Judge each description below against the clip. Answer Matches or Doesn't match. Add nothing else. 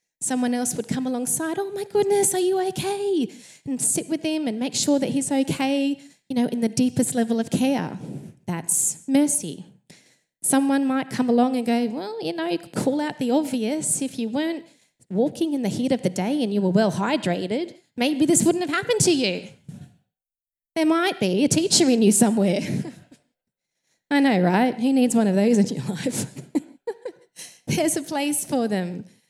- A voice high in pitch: Matches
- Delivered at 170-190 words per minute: Matches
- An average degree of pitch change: Matches